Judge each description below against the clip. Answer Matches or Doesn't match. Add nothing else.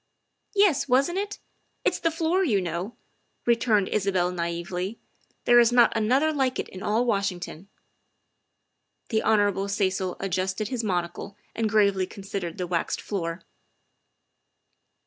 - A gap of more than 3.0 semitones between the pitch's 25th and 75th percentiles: Matches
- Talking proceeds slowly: Doesn't match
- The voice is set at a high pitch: Matches